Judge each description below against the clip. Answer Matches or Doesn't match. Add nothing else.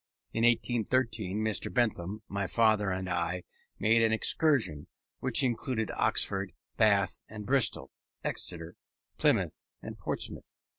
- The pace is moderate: Doesn't match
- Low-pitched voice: Matches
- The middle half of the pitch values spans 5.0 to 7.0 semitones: Doesn't match